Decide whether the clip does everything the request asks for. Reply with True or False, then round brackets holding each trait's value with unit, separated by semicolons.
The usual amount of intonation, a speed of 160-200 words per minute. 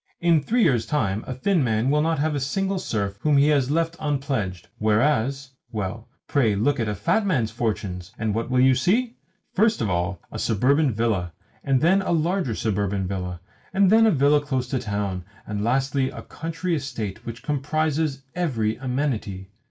False (6.2 semitones; 185 wpm)